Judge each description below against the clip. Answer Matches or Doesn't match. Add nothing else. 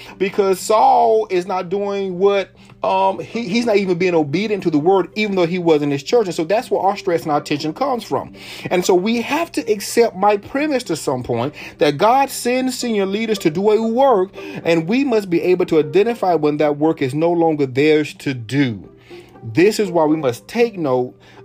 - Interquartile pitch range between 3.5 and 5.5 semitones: Matches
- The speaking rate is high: Matches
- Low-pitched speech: Doesn't match